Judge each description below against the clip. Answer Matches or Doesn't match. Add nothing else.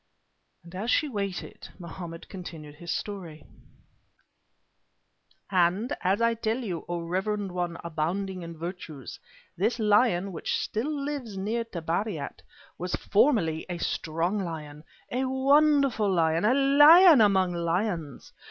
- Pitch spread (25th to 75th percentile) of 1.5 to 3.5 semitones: Doesn't match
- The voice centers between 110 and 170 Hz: Doesn't match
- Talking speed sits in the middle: Doesn't match